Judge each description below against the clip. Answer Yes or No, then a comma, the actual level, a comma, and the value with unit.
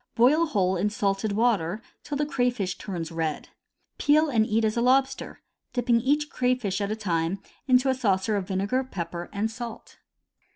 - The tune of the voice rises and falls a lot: No, average, 4.8 semitones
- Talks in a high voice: Yes, high, 220 Hz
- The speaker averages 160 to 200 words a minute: Yes, average, 170 wpm